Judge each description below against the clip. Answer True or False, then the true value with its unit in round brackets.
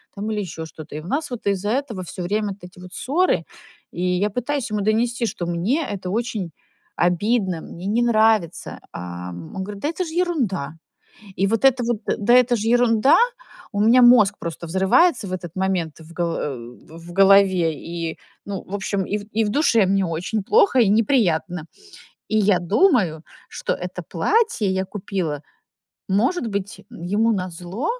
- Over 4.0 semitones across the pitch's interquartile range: True (4.8 semitones)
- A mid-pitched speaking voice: False (200 Hz)